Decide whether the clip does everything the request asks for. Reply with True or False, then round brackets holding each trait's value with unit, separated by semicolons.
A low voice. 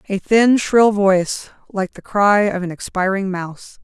False (195 Hz)